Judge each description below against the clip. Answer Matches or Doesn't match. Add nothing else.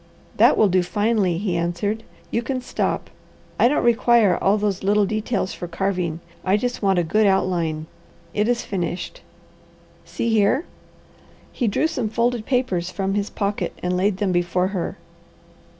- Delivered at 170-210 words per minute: Doesn't match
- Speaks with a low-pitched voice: Doesn't match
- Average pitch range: Matches